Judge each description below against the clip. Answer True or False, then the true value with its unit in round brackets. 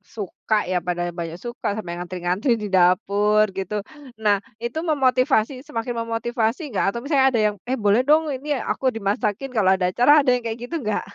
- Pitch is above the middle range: True (225 Hz)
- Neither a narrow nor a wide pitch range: True (4.2 semitones)